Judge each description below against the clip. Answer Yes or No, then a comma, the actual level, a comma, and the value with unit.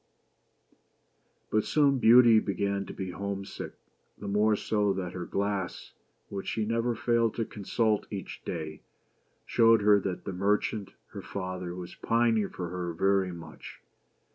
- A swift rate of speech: No, average, 145 wpm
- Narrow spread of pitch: No, average, 3.1 semitones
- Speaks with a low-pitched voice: Yes, low, 100 Hz